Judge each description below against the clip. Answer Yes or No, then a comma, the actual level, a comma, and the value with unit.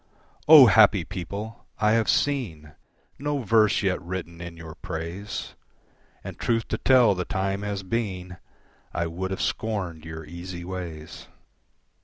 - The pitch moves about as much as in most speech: Yes, average, 4.2 semitones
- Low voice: Yes, very low, 95 Hz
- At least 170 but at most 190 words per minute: No, average, 140 wpm